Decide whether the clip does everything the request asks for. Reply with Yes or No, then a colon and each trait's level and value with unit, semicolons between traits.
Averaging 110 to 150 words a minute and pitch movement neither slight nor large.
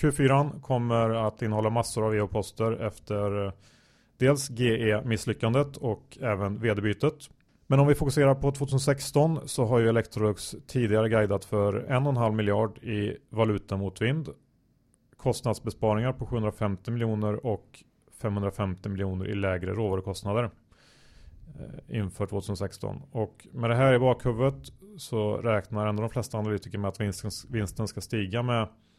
Yes: average, 135 wpm; average, 3.5 semitones